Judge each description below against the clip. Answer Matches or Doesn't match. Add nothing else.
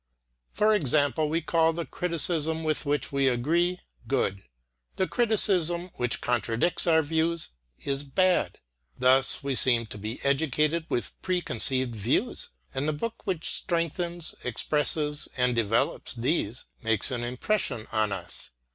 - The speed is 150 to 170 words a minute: Doesn't match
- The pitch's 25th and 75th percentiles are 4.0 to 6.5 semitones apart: Matches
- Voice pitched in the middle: Matches